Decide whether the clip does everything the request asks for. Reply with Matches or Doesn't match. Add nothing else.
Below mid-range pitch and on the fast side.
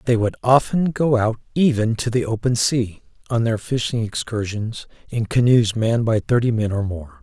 Doesn't match